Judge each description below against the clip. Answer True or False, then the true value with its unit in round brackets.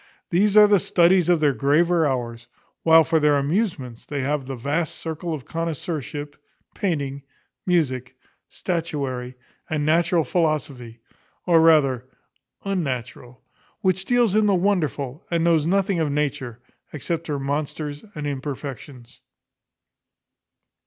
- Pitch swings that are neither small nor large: True (4.0 semitones)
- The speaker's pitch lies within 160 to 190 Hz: False (150 Hz)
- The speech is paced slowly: True (125 wpm)